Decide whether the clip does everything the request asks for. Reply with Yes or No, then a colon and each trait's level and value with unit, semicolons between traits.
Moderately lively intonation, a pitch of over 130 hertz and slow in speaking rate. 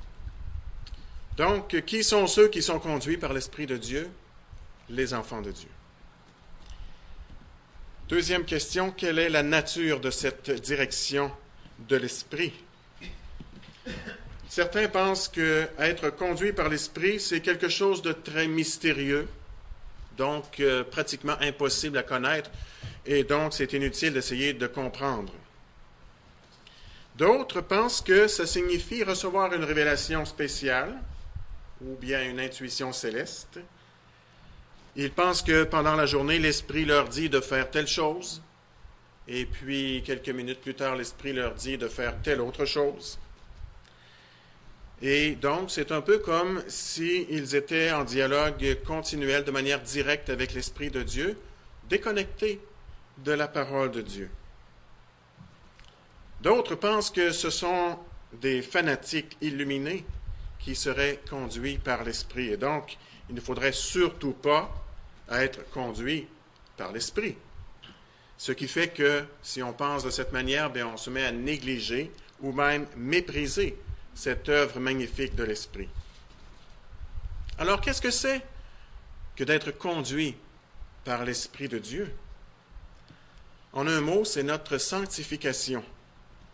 Yes: average, 4.9 semitones; medium, 140 Hz; slow, 125 wpm